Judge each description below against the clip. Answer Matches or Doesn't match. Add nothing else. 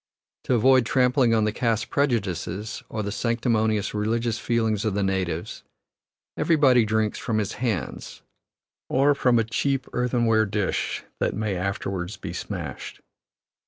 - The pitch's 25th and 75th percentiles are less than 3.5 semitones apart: Matches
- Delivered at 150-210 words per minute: Doesn't match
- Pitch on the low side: Matches